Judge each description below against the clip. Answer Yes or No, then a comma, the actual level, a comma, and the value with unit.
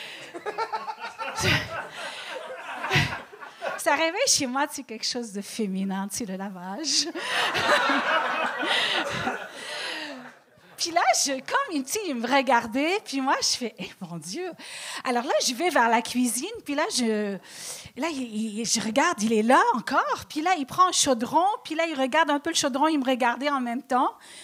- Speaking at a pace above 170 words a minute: No, average, 155 wpm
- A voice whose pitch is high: Yes, very high, 275 Hz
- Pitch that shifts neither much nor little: No, wide, 5.8 semitones